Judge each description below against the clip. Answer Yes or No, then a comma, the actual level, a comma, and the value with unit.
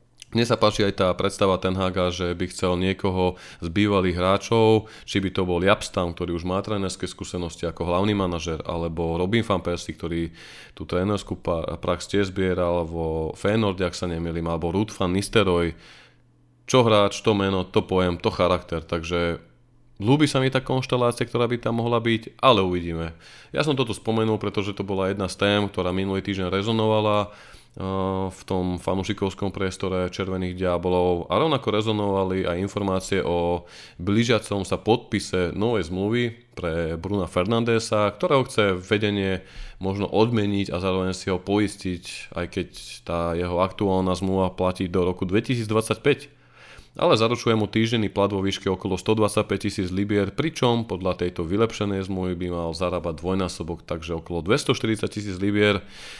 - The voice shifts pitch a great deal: No, average, 2.8 semitones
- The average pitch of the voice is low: Yes, very low, 95 Hz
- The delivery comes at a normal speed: Yes, average, 155 wpm